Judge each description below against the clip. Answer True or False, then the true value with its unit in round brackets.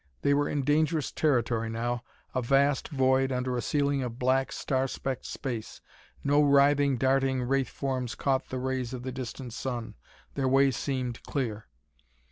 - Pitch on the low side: True (130 Hz)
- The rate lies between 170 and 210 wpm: False (160 wpm)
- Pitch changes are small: True (1.9 semitones)